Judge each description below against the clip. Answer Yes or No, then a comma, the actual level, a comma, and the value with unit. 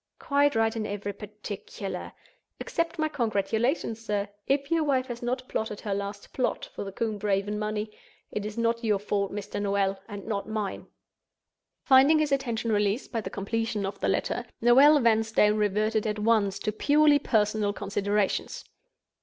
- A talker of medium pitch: No, high, 215 Hz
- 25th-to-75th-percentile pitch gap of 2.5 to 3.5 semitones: Yes, average, 2.9 semitones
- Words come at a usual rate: Yes, average, 160 wpm